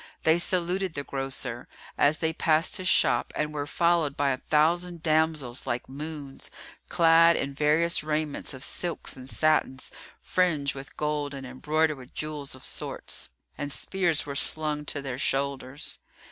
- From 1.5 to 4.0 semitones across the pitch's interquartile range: Yes, average, 2.7 semitones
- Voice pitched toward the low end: No, medium, 150 Hz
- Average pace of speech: Yes, average, 155 wpm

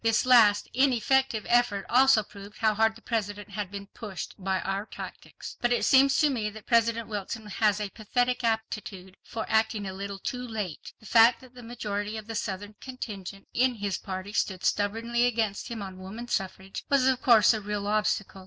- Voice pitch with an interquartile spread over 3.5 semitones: No, average, 2.9 semitones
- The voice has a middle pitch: No, high, 215 Hz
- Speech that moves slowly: No, average, 190 wpm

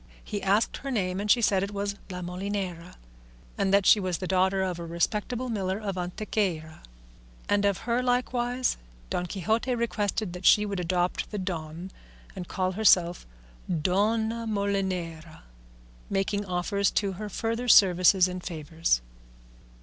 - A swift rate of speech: No, average, 150 wpm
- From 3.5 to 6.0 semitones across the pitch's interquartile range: No, average, 2.8 semitones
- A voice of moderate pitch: No, high, 195 Hz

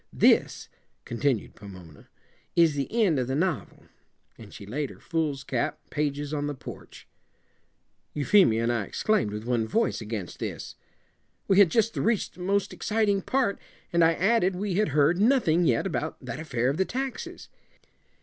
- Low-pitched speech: No, medium, 155 Hz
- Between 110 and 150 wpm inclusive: No, average, 160 wpm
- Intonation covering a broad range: Yes, wide, 8.3 semitones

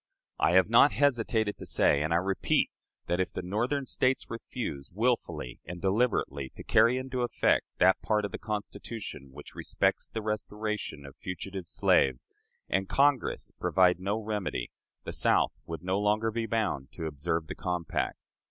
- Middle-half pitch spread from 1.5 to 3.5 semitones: No, average, 4.7 semitones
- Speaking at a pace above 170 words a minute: No, average, 160 wpm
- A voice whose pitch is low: Yes, low, 100 Hz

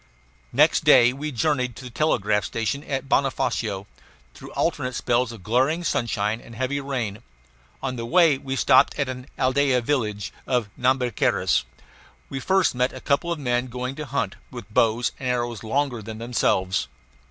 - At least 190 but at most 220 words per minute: No, average, 165 wpm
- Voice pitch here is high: No, low, 125 Hz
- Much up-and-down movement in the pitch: No, average, 3.0 semitones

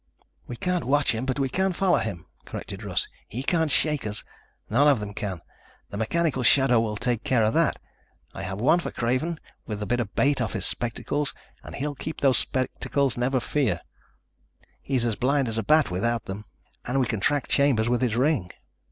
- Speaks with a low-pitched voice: Yes, low, 125 Hz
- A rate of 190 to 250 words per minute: Yes, average, 195 wpm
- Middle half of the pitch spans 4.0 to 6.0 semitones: Yes, average, 4.5 semitones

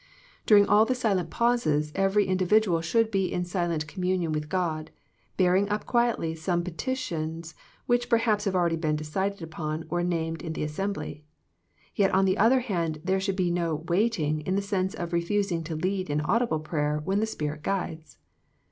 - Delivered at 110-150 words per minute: No, average, 185 wpm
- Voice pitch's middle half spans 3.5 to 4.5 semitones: Yes, average, 3.9 semitones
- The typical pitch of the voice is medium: Yes, medium, 180 Hz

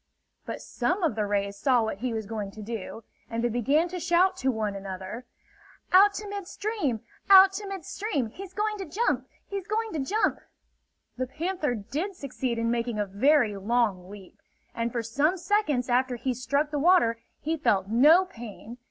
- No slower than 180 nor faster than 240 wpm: Yes, average, 185 wpm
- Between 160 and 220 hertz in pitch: No, very high, 260 Hz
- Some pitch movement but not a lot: No, wide, 8.5 semitones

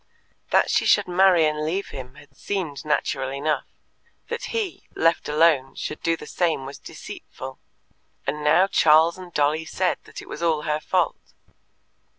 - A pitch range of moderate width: Yes, average, 3.0 semitones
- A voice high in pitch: No, medium, 155 Hz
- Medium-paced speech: Yes, average, 165 wpm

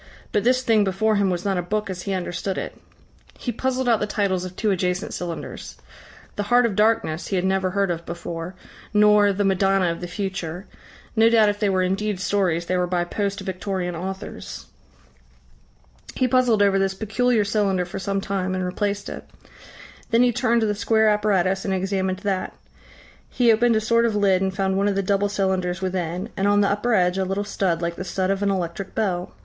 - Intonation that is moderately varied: No, narrow, 2.2 semitones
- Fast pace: Yes, fast, 210 wpm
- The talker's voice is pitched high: Yes, high, 195 Hz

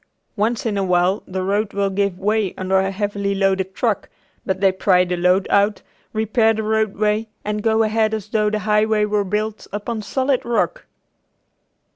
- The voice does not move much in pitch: Yes, narrow, 2.1 semitones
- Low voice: No, high, 210 Hz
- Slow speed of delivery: No, average, 170 wpm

